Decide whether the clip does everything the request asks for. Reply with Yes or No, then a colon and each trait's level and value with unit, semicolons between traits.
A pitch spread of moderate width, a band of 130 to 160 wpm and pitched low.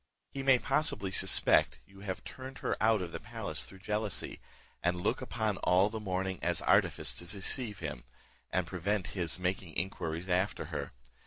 No: average, 3.1 semitones; average, 175 wpm; very low, 95 Hz